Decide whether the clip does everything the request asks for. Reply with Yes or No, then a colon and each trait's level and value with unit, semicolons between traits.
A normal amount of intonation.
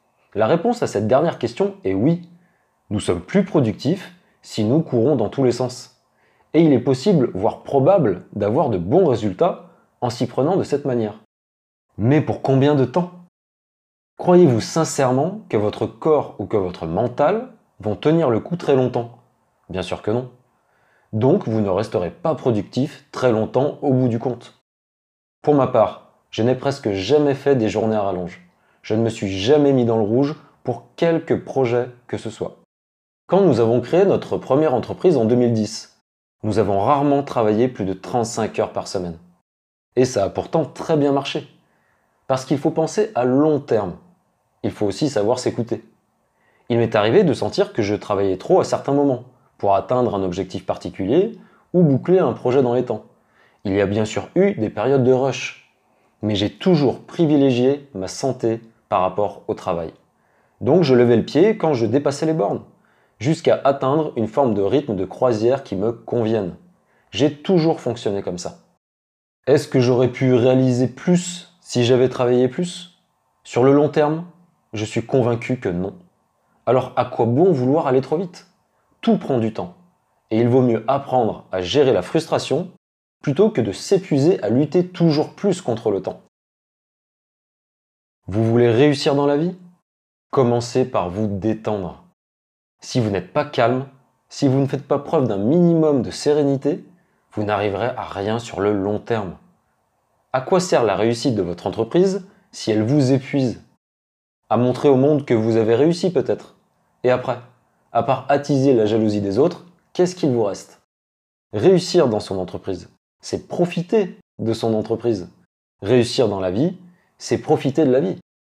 No: wide, 6.0 semitones